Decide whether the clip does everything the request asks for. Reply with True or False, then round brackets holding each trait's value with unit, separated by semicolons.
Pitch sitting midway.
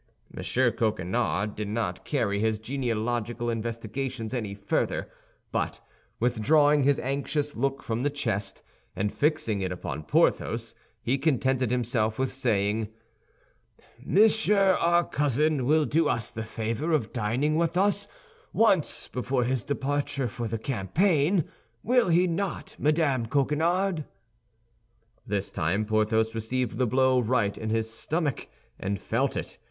False (125 Hz)